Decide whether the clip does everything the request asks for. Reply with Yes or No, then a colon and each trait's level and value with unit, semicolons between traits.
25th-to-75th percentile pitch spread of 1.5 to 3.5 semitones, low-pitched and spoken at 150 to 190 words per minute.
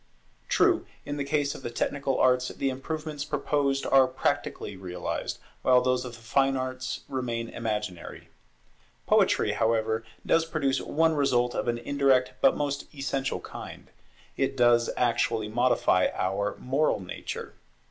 No: average, 2.9 semitones; low, 130 Hz; average, 140 wpm